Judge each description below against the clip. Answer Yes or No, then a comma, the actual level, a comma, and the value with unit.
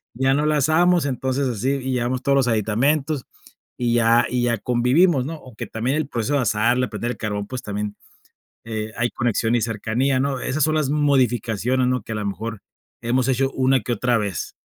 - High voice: No, low, 125 Hz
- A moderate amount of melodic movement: Yes, average, 3.1 semitones